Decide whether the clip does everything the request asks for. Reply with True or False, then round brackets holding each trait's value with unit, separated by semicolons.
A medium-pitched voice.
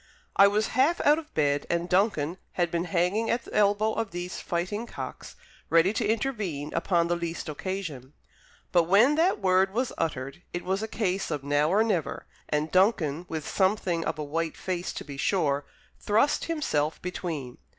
True (180 Hz)